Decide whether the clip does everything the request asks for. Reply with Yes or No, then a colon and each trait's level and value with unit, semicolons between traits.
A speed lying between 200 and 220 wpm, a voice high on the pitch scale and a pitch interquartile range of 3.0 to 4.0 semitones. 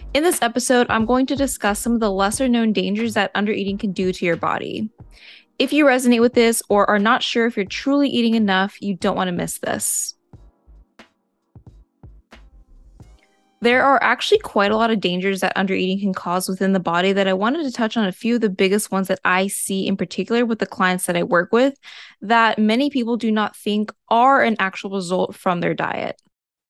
Yes: fast, 205 wpm; high, 210 Hz; average, 3.7 semitones